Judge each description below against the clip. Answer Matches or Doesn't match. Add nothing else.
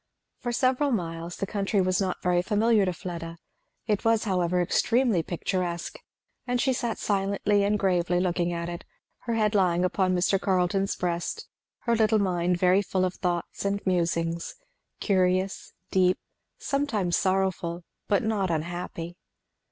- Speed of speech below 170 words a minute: Matches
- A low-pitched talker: Doesn't match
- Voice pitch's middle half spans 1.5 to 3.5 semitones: Matches